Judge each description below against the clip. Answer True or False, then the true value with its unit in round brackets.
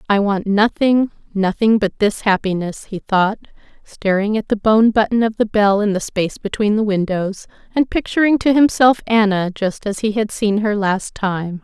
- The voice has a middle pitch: False (210 Hz)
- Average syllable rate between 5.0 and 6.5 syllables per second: False (4.7 syllables/s)